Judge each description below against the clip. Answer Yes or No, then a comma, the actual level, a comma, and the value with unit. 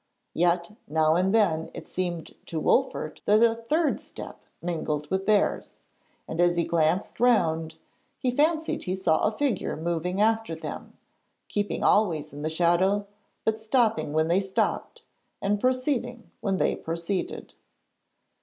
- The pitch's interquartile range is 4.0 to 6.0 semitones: Yes, average, 5.2 semitones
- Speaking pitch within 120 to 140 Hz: No, medium, 185 Hz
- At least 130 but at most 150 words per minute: Yes, average, 145 wpm